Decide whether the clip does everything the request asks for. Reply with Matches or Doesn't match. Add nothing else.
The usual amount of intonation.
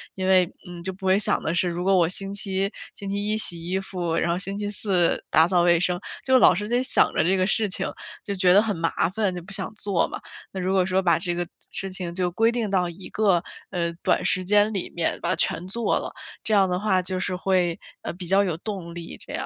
Doesn't match